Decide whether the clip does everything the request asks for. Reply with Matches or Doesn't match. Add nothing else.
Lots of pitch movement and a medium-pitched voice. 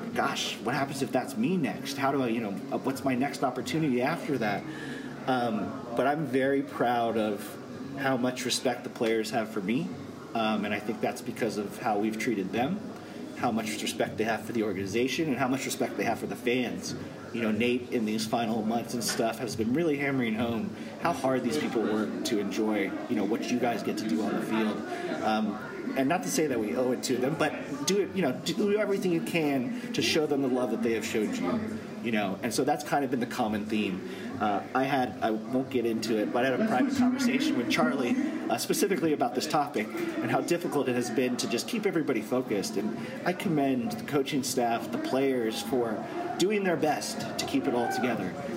Doesn't match